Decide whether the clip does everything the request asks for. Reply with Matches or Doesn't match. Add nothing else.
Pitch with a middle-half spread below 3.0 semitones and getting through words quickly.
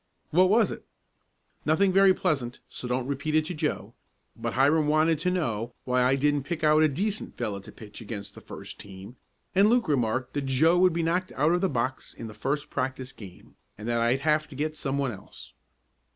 Doesn't match